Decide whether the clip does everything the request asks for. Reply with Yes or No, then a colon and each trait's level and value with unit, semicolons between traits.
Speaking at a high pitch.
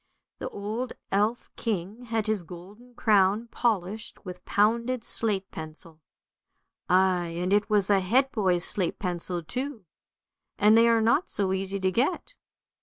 Yes: high, 205 Hz